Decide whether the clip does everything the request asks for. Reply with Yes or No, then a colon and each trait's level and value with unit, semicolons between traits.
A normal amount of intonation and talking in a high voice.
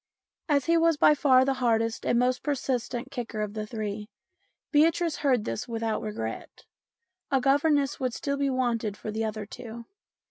Yes: average, 4.1 semitones; high, 245 Hz